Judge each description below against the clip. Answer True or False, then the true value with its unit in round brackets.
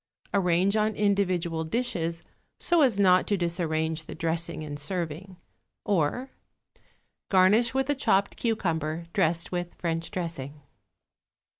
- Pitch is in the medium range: True (175 Hz)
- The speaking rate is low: True (120 wpm)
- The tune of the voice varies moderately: True (3.8 semitones)